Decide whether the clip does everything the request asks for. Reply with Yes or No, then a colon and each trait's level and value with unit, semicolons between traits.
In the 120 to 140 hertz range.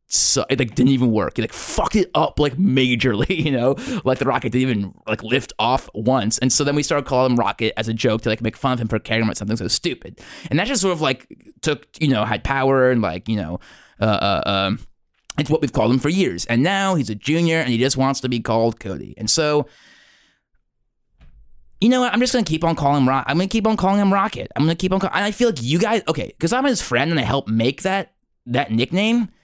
Yes: low, 135 Hz